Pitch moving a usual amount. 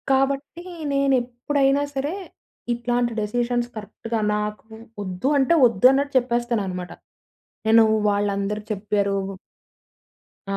Yes: average, 4.3 semitones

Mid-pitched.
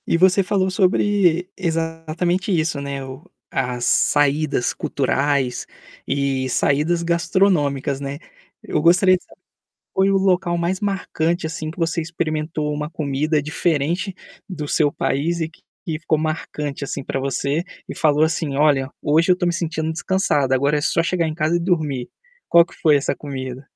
Yes: medium, 155 Hz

